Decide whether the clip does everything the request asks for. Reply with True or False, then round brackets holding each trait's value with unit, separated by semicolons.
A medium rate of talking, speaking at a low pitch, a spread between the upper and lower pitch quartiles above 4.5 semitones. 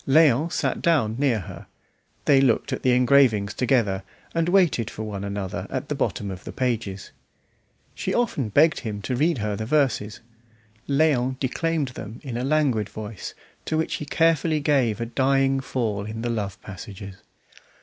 True (170 wpm; 125 Hz; 5.2 semitones)